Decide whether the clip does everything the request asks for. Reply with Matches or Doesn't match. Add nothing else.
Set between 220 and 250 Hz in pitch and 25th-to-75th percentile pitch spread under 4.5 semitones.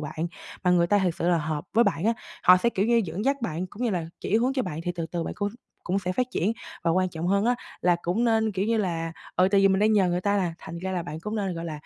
Doesn't match